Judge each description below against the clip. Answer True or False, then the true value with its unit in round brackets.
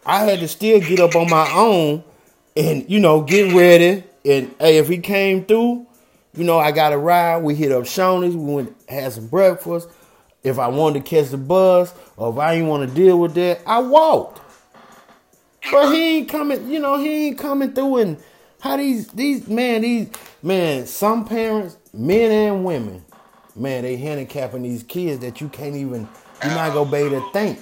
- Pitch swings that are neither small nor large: False (6.6 semitones)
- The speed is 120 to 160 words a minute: False (200 wpm)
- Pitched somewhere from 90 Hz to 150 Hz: False (175 Hz)